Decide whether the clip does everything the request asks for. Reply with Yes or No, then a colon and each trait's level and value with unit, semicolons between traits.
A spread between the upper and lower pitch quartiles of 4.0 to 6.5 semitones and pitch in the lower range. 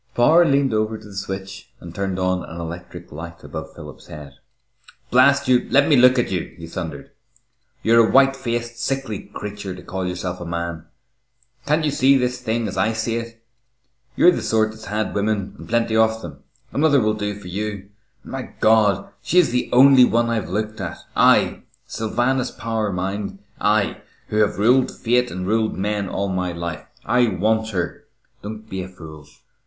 Yes: average, 4.4 semitones; low, 110 Hz